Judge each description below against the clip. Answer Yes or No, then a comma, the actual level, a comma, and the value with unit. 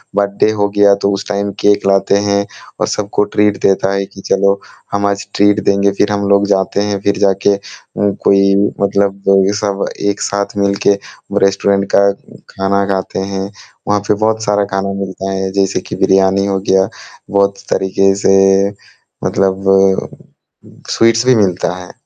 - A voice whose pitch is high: No, low, 100 Hz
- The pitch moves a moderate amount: No, narrow, 0.7 semitones